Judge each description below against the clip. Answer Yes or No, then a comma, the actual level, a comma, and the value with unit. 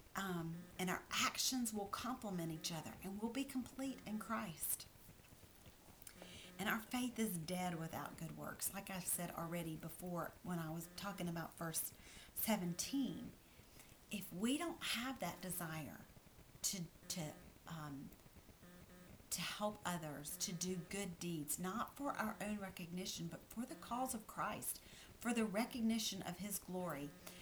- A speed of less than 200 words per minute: Yes, average, 145 wpm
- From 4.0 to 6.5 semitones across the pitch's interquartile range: Yes, average, 4.6 semitones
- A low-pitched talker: No, medium, 185 Hz